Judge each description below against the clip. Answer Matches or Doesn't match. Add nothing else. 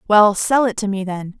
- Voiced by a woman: Matches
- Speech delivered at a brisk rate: Matches